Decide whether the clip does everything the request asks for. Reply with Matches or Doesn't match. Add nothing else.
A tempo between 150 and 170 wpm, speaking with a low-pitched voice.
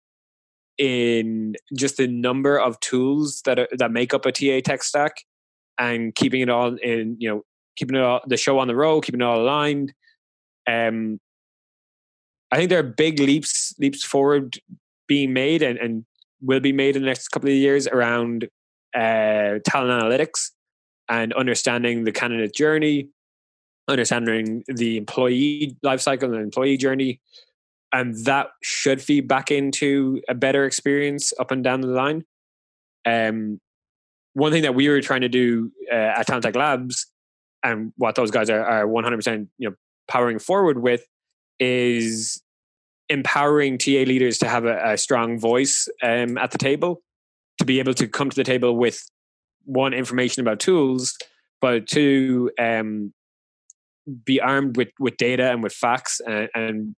Matches